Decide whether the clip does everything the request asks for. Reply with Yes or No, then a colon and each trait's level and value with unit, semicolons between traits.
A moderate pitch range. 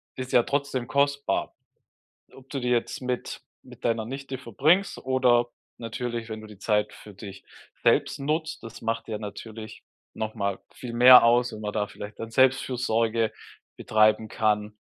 Yes: average, 3.1 semitones